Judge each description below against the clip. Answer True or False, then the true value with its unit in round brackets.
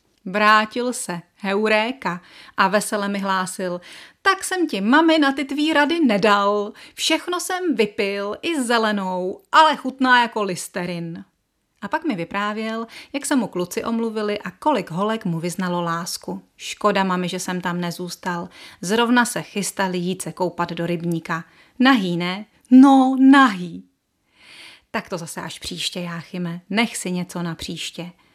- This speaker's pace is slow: False (145 wpm)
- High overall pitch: True (200 Hz)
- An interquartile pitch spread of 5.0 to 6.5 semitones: True (5.4 semitones)